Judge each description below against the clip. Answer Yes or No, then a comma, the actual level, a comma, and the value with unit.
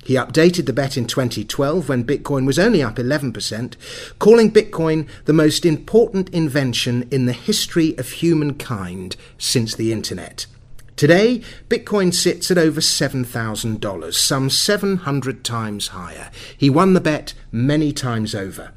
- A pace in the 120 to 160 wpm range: Yes, average, 140 wpm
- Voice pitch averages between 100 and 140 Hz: Yes, low, 135 Hz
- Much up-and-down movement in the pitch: Yes, wide, 5.7 semitones